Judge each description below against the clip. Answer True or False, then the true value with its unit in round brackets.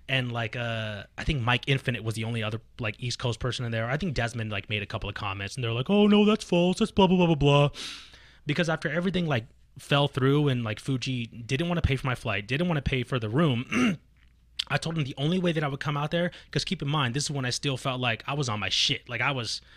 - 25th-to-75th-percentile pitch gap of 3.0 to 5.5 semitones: True (5.0 semitones)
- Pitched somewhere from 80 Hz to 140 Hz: True (135 Hz)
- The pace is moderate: False (280 wpm)